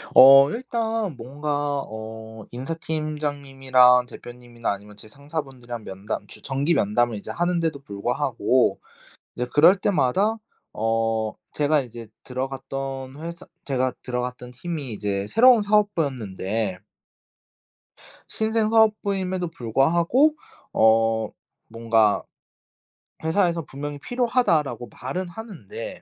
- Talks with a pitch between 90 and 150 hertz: Yes, low, 135 Hz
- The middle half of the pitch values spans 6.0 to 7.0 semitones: Yes, wide, 6.6 semitones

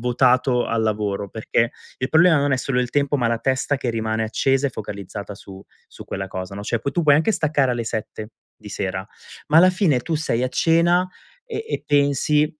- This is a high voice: No, low, 125 Hz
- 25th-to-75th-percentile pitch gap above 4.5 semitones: Yes, average, 5.0 semitones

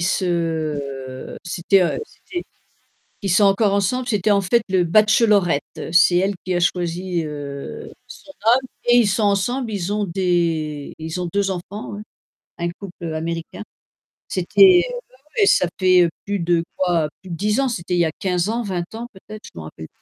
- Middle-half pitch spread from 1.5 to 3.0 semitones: No, average, 3.7 semitones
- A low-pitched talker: No, medium, 185 Hz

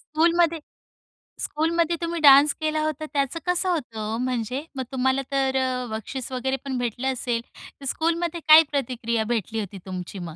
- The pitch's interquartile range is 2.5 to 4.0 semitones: No, average, 4.6 semitones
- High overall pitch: Yes, very high, 265 Hz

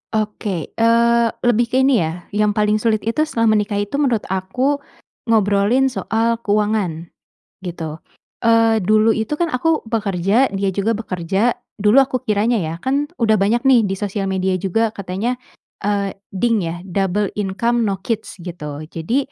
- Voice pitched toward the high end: Yes, high, 215 Hz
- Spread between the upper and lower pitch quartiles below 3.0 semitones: No, average, 3.3 semitones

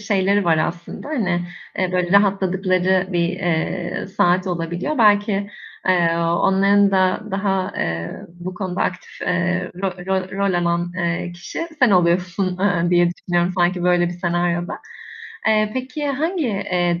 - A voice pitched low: No, medium, 185 Hz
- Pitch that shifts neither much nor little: No, narrow, 2.2 semitones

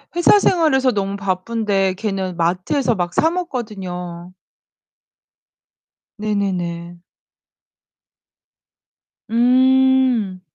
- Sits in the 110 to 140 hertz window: No, high, 200 Hz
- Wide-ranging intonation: Yes, wide, 5.9 semitones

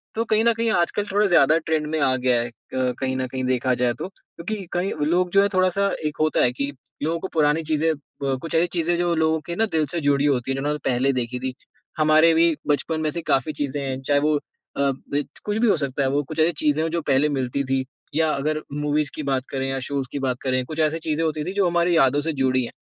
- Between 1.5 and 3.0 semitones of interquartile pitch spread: No, average, 3.7 semitones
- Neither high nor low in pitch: Yes, medium, 150 Hz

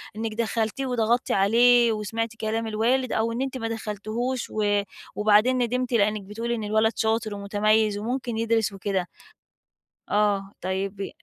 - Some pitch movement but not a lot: No, narrow, 2.1 semitones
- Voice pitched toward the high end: Yes, high, 220 Hz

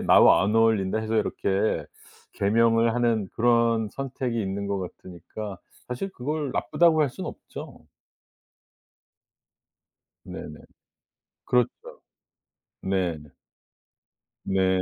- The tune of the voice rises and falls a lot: No, average, 3.8 semitones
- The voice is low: Yes, low, 110 Hz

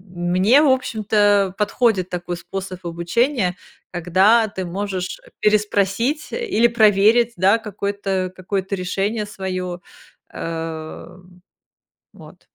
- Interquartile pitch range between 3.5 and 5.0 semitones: No, average, 3.0 semitones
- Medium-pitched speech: No, high, 195 Hz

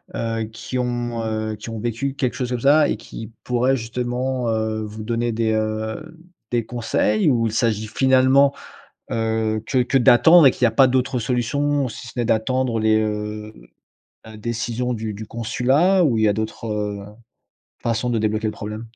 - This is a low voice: Yes, low, 115 Hz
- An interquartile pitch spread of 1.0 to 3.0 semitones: Yes, narrow, 2.5 semitones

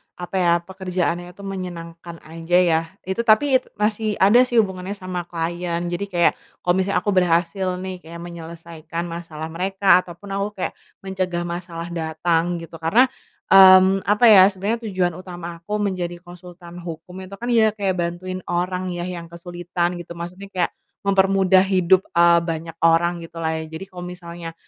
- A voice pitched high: No, medium, 180 Hz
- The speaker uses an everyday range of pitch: No, narrow, 2.1 semitones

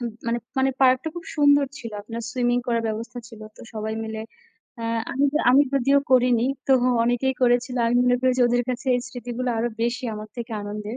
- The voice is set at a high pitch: Yes, high, 245 Hz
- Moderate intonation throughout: No, narrow, 1.8 semitones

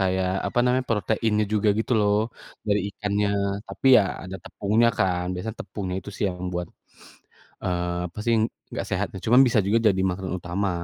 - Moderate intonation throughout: Yes, average, 3.0 semitones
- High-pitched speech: No, low, 100 Hz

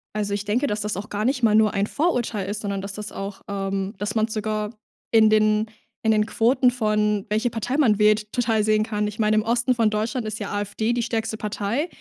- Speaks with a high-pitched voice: Yes, high, 215 Hz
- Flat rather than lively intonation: Yes, narrow, 1.5 semitones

